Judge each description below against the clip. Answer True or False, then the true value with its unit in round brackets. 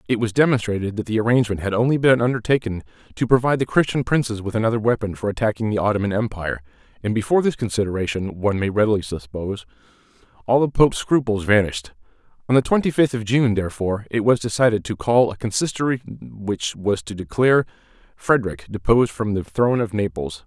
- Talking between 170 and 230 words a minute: True (180 wpm)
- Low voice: True (110 Hz)